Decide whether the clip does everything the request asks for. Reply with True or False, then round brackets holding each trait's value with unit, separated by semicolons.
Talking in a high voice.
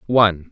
False (100 Hz)